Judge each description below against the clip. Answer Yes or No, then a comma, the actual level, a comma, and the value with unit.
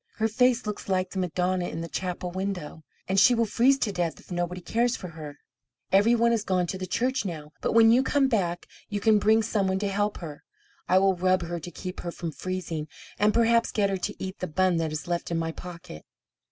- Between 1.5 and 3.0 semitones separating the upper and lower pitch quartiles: No, average, 3.8 semitones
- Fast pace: Yes, fast, 235 wpm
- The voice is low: No, medium, 185 Hz